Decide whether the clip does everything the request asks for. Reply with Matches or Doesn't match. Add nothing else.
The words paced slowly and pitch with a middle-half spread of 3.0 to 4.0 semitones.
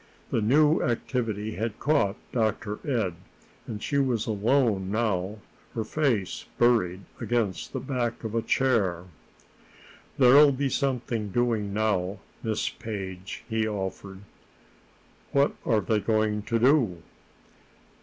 Matches